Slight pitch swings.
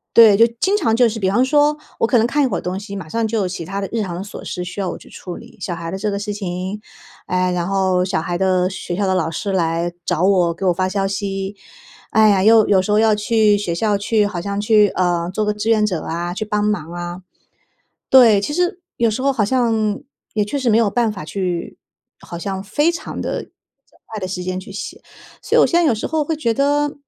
No: average, 3.4 semitones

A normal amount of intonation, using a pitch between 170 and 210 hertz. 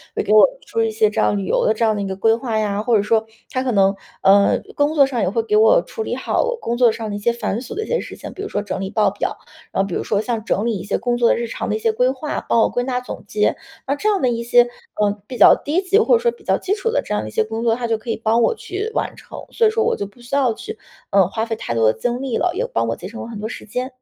No: average, 3.9 semitones; high, 230 Hz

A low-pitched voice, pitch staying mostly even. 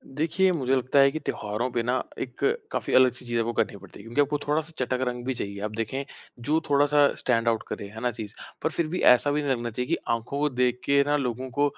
No: low, 125 Hz; average, 3.6 semitones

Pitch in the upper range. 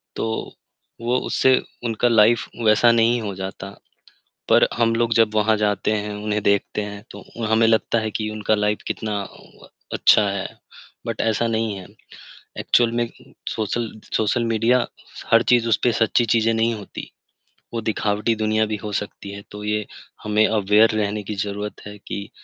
No: low, 110 Hz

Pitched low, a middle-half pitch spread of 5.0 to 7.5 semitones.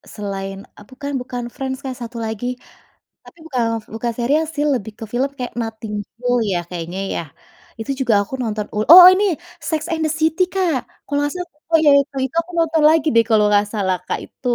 No: very high, 250 Hz; wide, 5.6 semitones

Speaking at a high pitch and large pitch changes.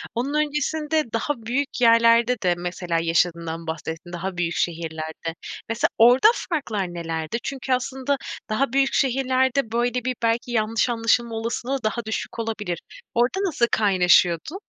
Yes: high, 230 Hz; wide, 6.6 semitones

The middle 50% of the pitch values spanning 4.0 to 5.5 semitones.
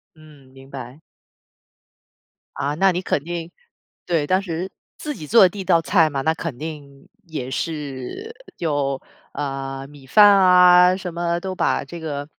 Yes: average, 4.3 semitones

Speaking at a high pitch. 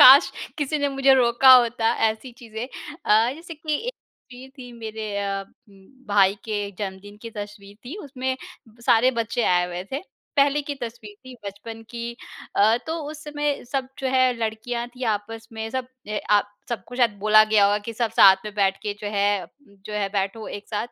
Yes: high, 225 Hz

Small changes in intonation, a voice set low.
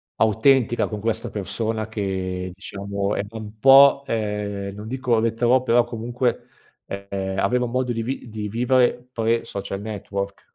No: average, 3.4 semitones; low, 110 Hz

